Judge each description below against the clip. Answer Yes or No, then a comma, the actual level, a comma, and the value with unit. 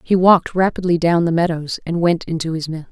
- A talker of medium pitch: Yes, medium, 170 Hz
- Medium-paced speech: No, fast, 225 wpm